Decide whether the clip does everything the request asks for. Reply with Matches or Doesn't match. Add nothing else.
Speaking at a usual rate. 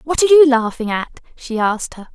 Doesn't match